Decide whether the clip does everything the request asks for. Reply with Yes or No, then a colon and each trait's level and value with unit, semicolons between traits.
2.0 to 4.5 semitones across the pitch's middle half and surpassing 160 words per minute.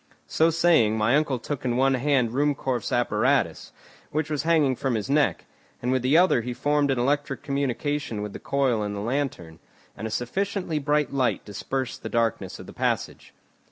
Yes: average, 3.6 semitones; average, 185 wpm